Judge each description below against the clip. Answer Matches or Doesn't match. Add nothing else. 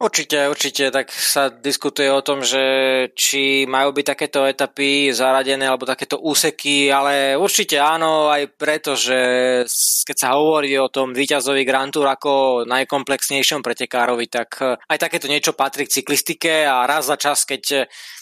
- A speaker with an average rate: Matches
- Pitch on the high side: Doesn't match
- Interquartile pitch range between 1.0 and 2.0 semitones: Matches